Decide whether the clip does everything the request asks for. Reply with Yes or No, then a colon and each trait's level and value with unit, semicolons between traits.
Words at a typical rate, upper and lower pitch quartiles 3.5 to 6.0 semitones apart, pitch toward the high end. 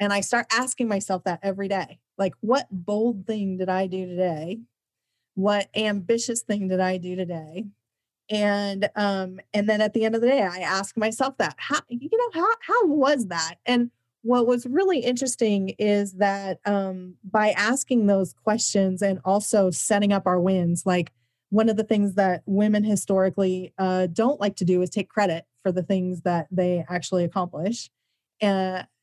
No: average, 180 wpm; average, 3.0 semitones; high, 200 Hz